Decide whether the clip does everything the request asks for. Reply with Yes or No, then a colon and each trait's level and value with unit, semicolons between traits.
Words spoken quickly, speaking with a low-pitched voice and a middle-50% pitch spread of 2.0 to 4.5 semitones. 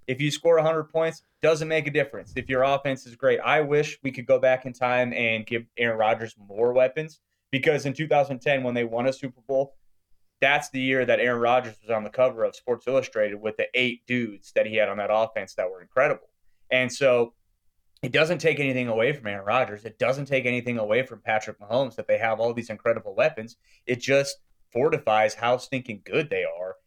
Yes: fast, 215 wpm; low, 125 Hz; average, 3.9 semitones